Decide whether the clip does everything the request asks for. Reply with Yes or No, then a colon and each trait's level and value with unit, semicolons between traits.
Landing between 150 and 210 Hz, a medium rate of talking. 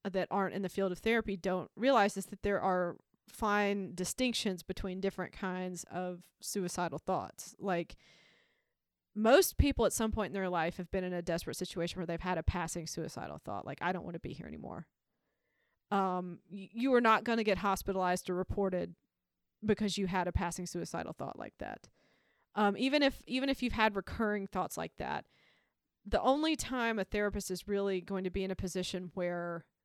Yes: high, 190 Hz; average, 195 wpm